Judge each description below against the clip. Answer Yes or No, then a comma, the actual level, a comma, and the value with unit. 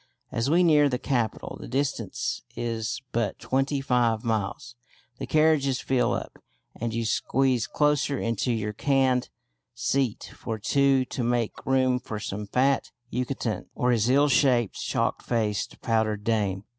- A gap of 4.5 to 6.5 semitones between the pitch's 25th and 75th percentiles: No, average, 3.3 semitones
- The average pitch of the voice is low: Yes, low, 125 Hz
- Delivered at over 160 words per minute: No, average, 145 wpm